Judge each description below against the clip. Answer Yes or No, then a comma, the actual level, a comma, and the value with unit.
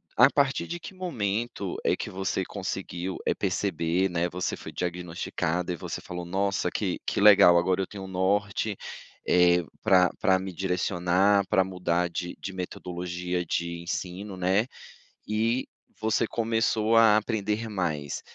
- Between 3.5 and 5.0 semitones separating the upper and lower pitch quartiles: No, average, 2.8 semitones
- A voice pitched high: No, very low, 95 Hz